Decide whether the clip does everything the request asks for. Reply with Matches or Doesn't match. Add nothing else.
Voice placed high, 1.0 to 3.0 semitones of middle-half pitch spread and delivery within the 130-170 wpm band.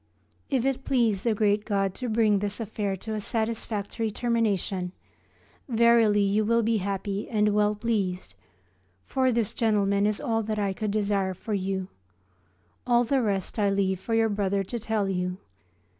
Matches